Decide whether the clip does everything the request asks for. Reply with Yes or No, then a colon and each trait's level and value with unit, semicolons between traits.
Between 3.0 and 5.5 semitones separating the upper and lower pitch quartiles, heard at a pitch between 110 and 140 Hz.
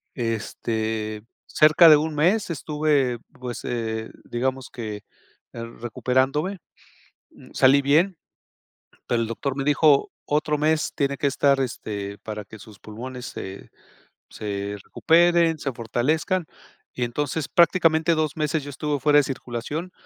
Yes: average, 4.8 semitones; low, 135 Hz